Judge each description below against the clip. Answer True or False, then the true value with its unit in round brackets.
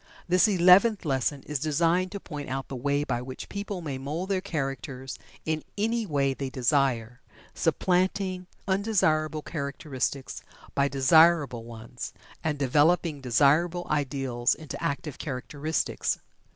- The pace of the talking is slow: True (125 wpm)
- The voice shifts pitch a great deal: False (4.7 semitones)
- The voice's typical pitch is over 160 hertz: False (145 Hz)